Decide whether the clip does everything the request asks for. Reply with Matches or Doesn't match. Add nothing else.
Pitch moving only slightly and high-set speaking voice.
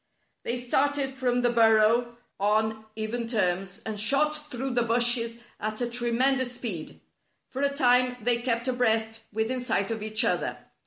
Matches